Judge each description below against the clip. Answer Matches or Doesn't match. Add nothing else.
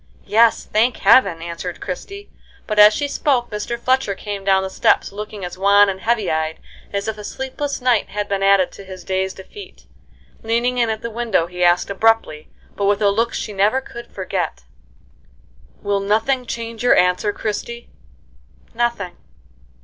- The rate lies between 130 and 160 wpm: Doesn't match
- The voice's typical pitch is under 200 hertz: Doesn't match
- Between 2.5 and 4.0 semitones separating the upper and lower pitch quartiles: Matches